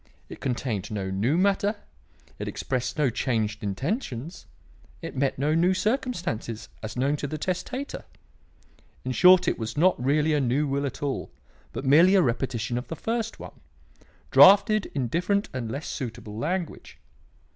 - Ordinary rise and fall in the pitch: No, wide, 7.2 semitones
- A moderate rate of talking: Yes, average, 155 wpm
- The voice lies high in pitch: No, medium, 140 Hz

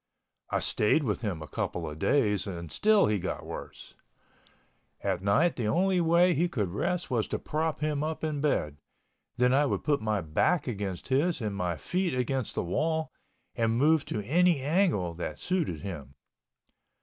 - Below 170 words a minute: No, average, 175 wpm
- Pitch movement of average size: No, wide, 8.5 semitones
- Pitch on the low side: Yes, low, 130 Hz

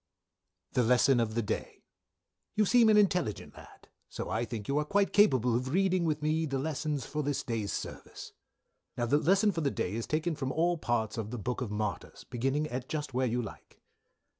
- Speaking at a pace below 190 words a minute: No, fast, 205 wpm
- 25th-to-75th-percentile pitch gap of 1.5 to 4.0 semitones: No, average, 5.2 semitones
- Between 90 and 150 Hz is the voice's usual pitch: Yes, low, 135 Hz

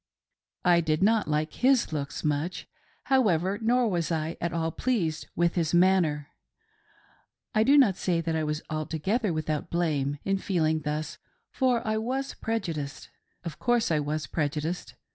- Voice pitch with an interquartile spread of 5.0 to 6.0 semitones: Yes, wide, 5.6 semitones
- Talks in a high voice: No, medium, 170 Hz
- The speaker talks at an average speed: Yes, average, 155 wpm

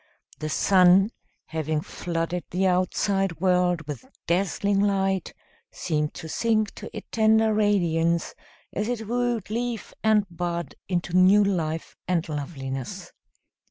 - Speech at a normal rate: No, slow, 125 wpm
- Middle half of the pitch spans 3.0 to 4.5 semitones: Yes, average, 3.8 semitones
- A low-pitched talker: No, medium, 185 Hz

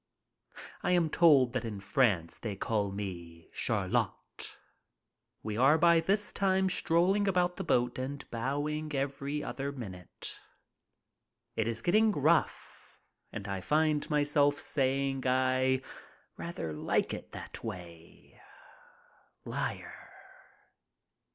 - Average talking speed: No, slow, 110 wpm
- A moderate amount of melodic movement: No, wide, 6.2 semitones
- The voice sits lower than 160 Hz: Yes, low, 135 Hz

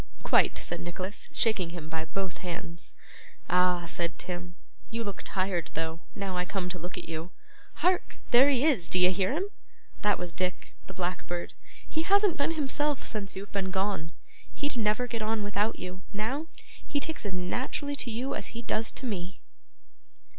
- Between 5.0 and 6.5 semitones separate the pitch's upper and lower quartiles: Yes, average, 5.3 semitones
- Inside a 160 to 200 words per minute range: Yes, average, 175 wpm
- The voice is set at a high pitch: Yes, high, 195 Hz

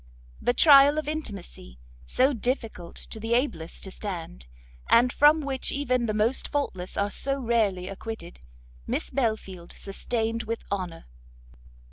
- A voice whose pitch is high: Yes, high, 225 Hz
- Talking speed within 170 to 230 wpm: No, slow, 135 wpm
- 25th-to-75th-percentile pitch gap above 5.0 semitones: Yes, wide, 5.6 semitones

